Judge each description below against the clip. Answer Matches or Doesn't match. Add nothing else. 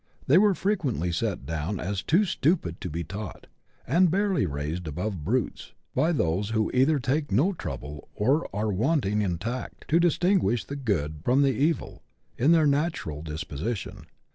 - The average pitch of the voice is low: Matches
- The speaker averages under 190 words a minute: Matches